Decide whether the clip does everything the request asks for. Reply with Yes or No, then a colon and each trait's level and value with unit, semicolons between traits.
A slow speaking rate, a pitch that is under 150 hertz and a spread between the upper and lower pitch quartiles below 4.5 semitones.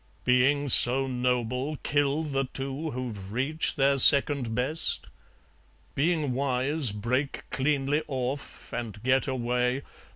Yes: slow, 110 wpm; low, 135 Hz; narrow, 2.4 semitones